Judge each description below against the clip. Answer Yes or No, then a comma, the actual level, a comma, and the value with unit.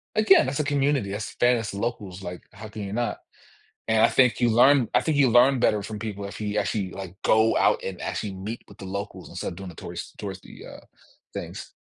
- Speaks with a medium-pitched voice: No, low, 110 Hz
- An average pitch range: Yes, average, 3.6 semitones